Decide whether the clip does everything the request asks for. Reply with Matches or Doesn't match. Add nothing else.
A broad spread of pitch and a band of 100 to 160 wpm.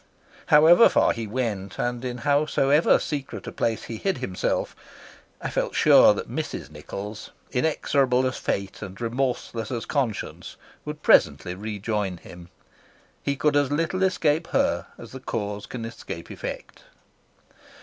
Matches